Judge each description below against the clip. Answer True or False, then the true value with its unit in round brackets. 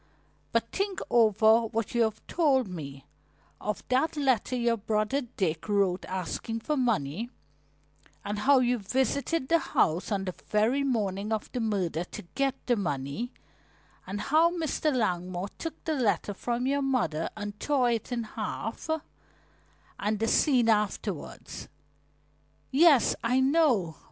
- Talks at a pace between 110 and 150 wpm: True (140 wpm)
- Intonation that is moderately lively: True (4.8 semitones)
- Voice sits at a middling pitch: False (225 Hz)